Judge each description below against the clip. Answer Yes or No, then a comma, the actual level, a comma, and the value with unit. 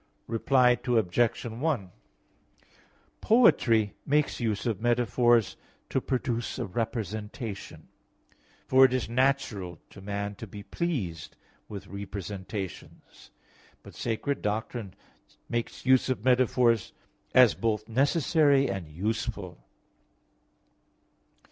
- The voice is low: Yes, low, 115 Hz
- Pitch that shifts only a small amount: No, average, 4.0 semitones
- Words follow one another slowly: Yes, slow, 100 wpm